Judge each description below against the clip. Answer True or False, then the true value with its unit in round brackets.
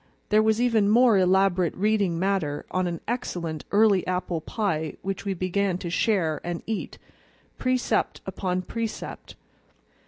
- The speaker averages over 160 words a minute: False (135 wpm)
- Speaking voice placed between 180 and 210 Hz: True (190 Hz)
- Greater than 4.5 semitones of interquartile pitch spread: False (3.5 semitones)